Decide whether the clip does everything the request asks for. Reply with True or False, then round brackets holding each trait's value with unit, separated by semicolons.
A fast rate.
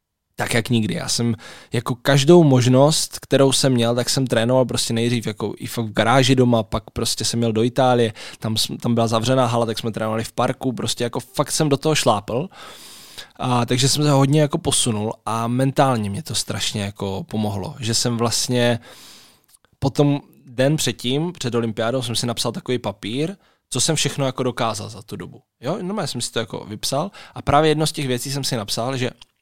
True (205 wpm)